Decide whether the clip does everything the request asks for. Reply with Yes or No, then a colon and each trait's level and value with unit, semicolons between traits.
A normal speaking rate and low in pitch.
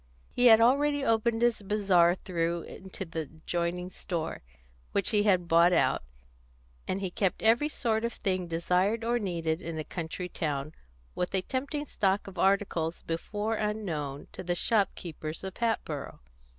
No: average, 155 wpm; medium, 185 Hz